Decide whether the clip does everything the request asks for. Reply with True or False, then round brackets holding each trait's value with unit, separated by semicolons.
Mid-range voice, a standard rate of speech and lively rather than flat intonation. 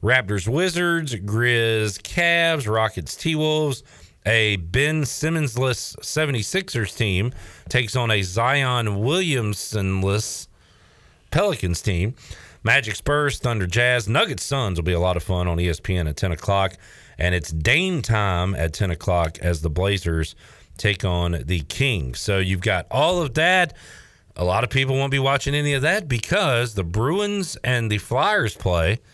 False (110 Hz; 150 wpm; 6.6 semitones)